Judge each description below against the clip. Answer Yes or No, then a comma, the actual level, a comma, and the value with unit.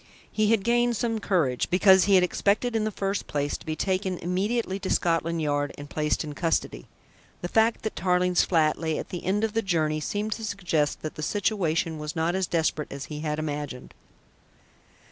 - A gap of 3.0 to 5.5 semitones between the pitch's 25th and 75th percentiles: Yes, average, 4.9 semitones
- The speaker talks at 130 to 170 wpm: No, average, 200 wpm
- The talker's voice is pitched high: No, medium, 180 Hz